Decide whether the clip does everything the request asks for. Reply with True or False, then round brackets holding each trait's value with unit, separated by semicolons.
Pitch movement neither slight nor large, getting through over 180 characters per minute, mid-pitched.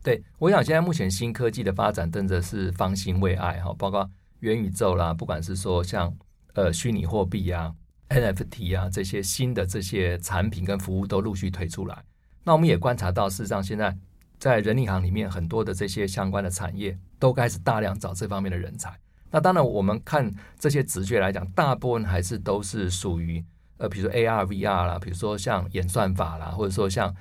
False (3.0 semitones; 310 characters per minute; 100 Hz)